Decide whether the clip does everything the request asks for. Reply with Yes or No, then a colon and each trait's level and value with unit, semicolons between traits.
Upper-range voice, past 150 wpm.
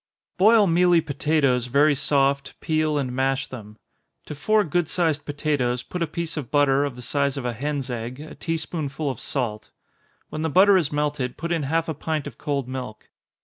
No: medium, 145 Hz; average, 200 wpm